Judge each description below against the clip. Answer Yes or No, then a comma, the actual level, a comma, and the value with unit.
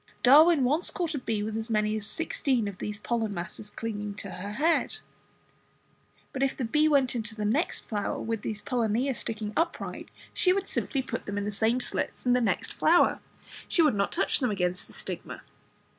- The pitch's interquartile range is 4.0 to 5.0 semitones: Yes, average, 4.6 semitones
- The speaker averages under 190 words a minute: No, average, 200 wpm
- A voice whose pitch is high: Yes, high, 225 Hz